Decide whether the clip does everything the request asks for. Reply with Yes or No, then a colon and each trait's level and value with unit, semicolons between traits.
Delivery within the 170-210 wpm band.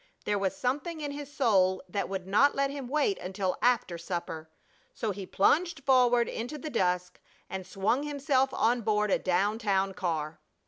Yes: average, 175 wpm